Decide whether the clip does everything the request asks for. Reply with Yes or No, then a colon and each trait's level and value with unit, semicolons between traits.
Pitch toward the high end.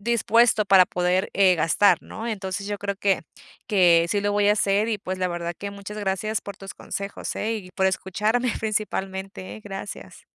Yes: high, 200 Hz